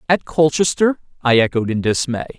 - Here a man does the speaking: Yes, male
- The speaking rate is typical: Yes, average, 150 wpm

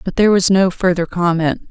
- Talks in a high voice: No, medium, 180 Hz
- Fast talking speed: Yes, fast, 210 wpm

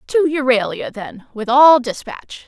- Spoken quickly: No, average, 145 wpm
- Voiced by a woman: Yes, female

